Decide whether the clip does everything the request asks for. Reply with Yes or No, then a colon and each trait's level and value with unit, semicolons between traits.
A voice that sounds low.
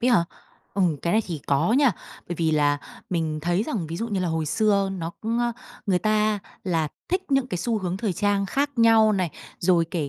No: high, 195 Hz